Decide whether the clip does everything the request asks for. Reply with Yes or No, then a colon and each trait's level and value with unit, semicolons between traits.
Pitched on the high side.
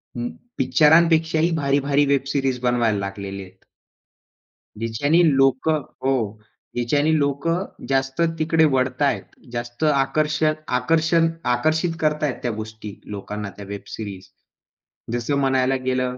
No: low, 135 Hz